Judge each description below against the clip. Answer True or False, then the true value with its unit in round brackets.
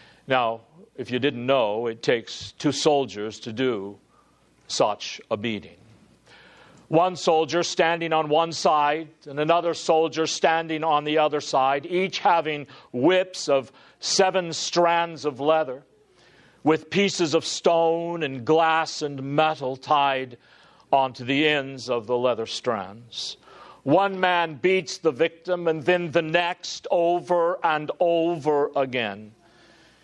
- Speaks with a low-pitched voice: False (155 Hz)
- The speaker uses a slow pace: True (130 wpm)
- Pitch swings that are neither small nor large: True (4.2 semitones)